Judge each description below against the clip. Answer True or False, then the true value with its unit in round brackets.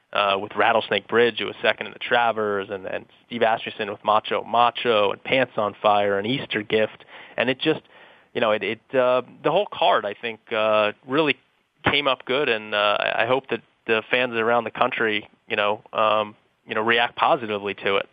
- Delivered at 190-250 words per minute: True (200 wpm)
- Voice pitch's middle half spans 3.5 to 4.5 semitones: False (3.1 semitones)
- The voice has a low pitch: True (110 Hz)